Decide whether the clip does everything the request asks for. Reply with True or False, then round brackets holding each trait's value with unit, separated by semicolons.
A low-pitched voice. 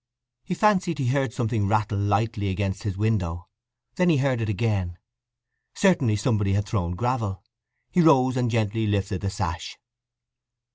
True (110 Hz)